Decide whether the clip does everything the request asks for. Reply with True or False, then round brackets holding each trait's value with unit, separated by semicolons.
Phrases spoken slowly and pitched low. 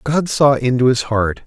False (205 wpm; 130 Hz)